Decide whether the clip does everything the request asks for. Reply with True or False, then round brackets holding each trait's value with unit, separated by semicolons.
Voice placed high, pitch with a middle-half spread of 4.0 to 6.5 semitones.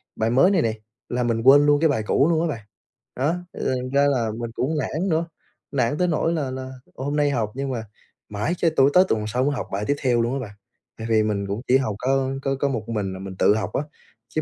False (130 Hz; 4.3 semitones)